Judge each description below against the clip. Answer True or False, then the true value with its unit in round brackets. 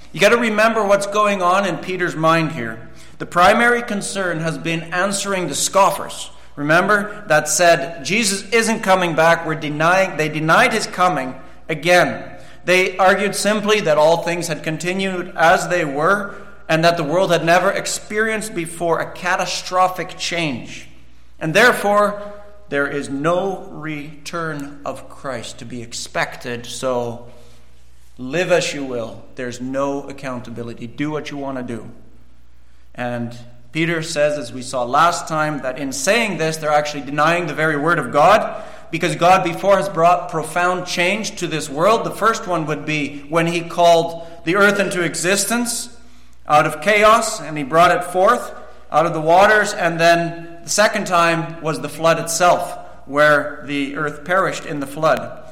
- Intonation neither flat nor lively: True (4.2 semitones)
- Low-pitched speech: False (170 Hz)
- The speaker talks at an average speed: True (160 wpm)